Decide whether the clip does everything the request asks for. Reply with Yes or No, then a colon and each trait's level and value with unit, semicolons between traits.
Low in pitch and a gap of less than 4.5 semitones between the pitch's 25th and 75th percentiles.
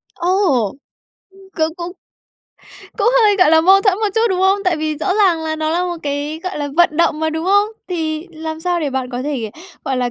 No: very high, 325 Hz; average, 3.5 semitones